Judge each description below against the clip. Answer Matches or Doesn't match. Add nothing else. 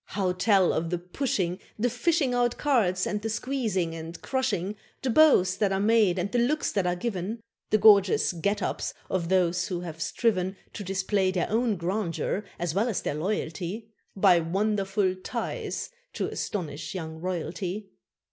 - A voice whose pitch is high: Matches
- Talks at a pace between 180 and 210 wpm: Doesn't match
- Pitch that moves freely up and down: Doesn't match